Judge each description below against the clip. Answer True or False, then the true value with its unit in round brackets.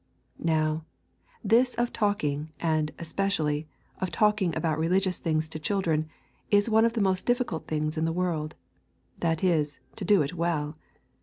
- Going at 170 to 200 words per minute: False (155 wpm)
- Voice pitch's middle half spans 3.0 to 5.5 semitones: True (4.2 semitones)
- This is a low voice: False (165 Hz)